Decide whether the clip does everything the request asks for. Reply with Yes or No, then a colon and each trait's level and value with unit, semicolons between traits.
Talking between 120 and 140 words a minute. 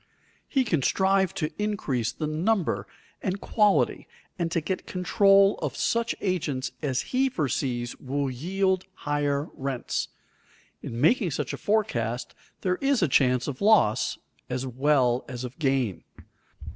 Yes: slow, 135 wpm